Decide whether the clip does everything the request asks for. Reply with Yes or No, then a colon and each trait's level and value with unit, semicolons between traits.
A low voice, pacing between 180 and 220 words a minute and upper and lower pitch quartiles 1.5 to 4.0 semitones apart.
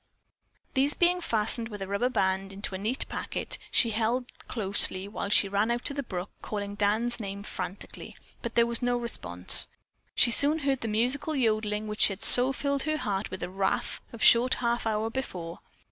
No: high, 225 Hz; average, 185 wpm; average, 3.6 semitones